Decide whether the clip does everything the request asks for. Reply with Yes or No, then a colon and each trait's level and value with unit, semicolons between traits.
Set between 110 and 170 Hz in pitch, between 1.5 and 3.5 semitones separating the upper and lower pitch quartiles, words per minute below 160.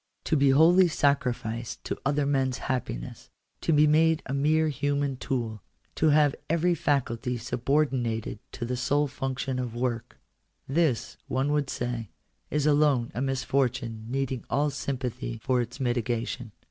Yes: low, 135 Hz; average, 3.2 semitones; average, 145 wpm